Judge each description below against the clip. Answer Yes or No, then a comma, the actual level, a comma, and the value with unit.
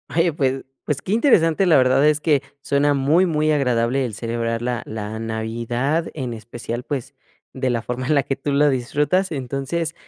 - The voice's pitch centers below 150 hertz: Yes, low, 135 Hz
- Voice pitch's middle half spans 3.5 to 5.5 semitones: Yes, average, 4.1 semitones